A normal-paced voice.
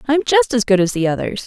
No: fast, 330 wpm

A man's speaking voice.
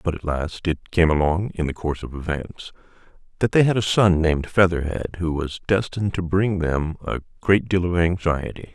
Yes: male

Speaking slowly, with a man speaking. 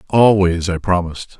Yes: slow, 130 wpm; male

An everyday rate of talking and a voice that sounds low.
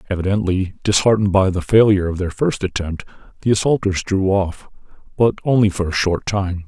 Yes: average, 170 wpm; very low, 95 Hz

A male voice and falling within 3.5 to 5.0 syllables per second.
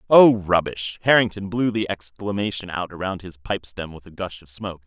No: male; 5.2 syllables/s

